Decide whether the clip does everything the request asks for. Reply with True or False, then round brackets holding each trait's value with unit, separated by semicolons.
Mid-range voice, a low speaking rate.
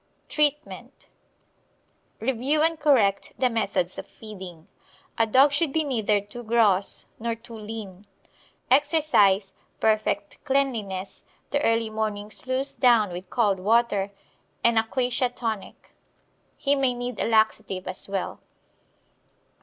False (225 Hz; 120 wpm)